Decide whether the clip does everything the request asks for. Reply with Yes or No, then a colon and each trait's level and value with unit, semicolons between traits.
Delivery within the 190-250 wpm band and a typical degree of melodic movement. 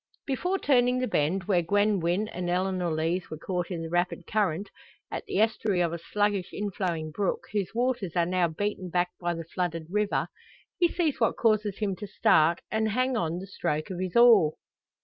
Yes: average, 195 wpm; average, 3.8 semitones